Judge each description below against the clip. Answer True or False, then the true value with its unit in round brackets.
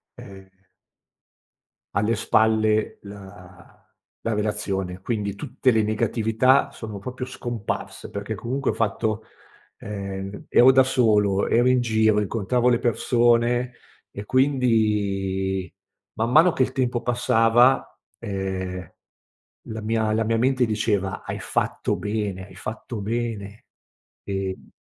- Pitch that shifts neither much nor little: True (3.2 semitones)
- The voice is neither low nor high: False (110 Hz)